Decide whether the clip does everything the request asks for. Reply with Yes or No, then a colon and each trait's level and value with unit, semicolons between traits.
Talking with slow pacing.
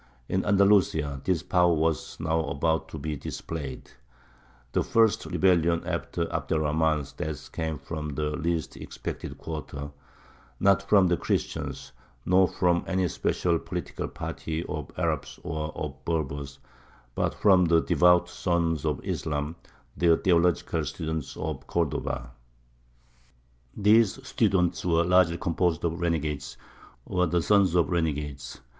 Yes: slow, 130 wpm